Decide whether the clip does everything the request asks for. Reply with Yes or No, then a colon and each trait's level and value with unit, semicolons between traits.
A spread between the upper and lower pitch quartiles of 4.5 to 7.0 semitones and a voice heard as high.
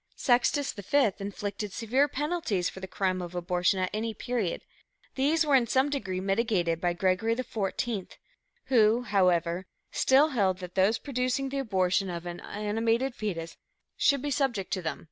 Yes: wide, 5.6 semitones; high, 210 Hz